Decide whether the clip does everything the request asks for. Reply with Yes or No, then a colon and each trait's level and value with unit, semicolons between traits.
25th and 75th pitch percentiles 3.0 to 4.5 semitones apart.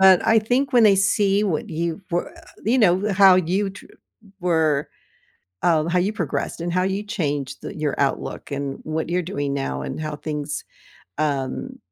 No: average, 4.9 semitones